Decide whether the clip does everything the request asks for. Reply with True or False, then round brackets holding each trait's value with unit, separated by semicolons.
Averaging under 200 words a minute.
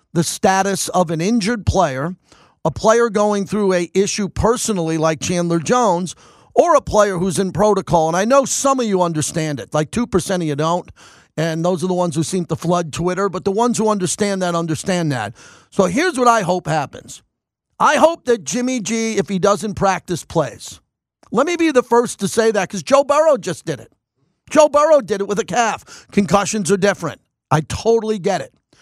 False (205 wpm)